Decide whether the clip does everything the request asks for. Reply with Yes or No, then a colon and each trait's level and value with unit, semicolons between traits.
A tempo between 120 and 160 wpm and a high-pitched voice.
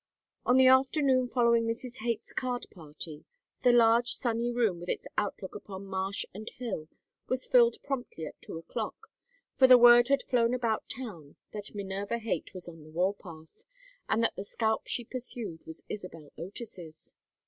No: average, 170 wpm; high, 225 Hz